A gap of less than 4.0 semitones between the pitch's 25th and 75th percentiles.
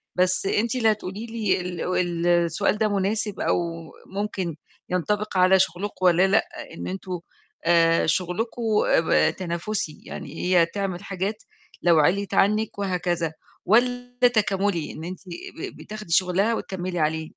Yes: average, 3.3 semitones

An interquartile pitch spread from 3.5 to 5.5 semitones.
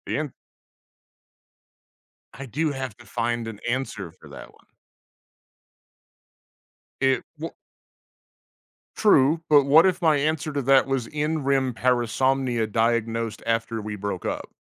Yes: average, 4.1 semitones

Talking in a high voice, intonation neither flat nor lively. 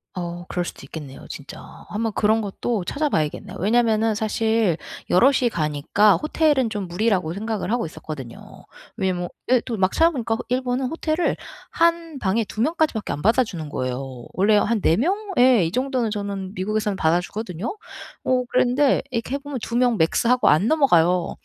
No: high, 220 Hz; wide, 5.9 semitones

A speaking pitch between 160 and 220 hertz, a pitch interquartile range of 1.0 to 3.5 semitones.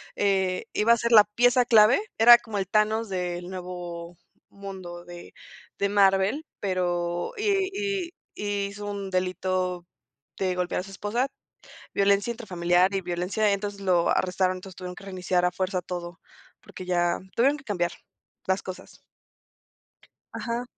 Yes: high, 190 Hz; average, 2.8 semitones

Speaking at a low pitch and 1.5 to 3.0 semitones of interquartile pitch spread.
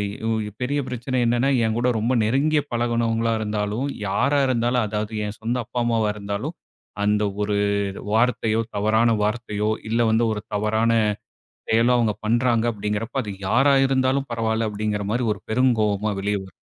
Yes: low, 115 Hz; average, 2.7 semitones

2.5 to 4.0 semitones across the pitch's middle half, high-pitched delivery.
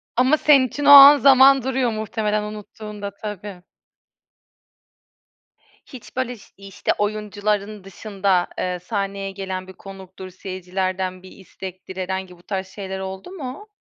Yes: average, 3.6 semitones; high, 200 Hz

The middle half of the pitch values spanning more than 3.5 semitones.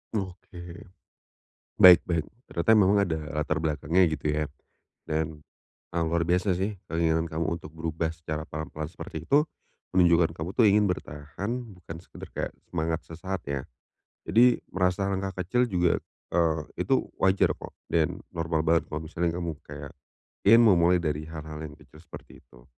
No: average, 2.7 semitones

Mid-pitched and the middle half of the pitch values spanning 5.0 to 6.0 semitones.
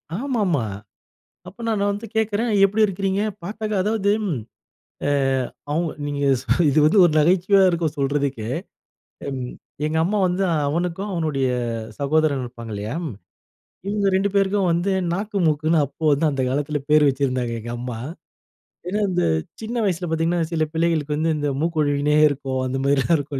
Yes: medium, 160 Hz; wide, 5.5 semitones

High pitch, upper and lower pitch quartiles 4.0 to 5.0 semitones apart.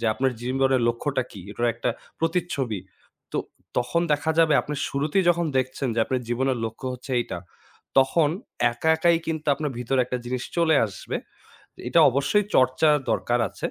No: low, 135 Hz; average, 4.3 semitones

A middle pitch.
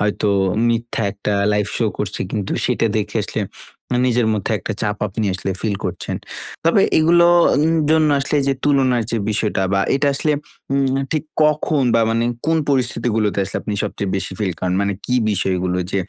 No: low, 115 Hz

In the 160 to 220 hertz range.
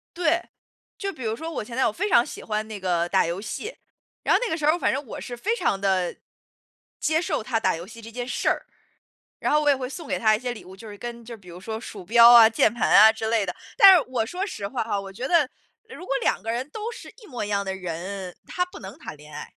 No: high, 230 Hz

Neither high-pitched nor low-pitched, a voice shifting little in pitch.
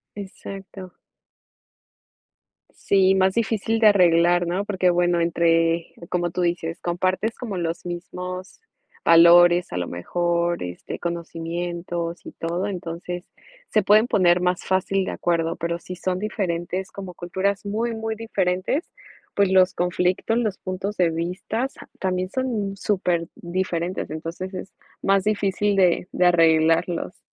Yes: medium, 180 Hz; narrow, 2.3 semitones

